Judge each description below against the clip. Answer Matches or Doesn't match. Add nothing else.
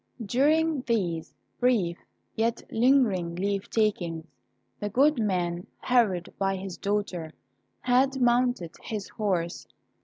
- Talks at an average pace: Doesn't match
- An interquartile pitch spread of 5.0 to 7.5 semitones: Matches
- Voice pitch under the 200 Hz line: Doesn't match